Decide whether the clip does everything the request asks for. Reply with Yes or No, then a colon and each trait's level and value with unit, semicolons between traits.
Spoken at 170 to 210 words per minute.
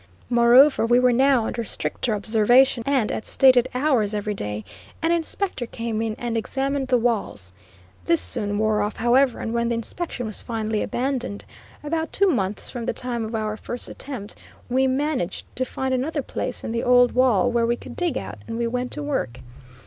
Yes: average, 190 wpm